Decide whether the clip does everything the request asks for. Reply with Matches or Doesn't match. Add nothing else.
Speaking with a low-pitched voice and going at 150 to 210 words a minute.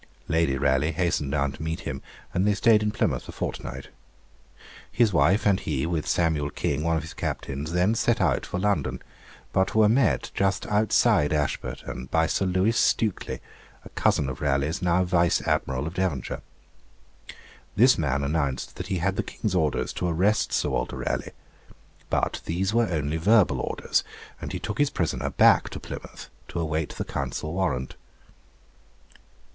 Matches